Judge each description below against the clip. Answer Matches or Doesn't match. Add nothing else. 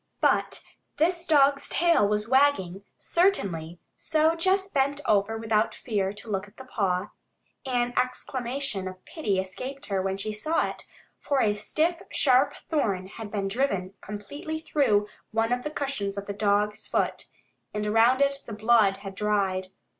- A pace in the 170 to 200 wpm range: Doesn't match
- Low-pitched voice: Doesn't match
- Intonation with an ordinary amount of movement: Doesn't match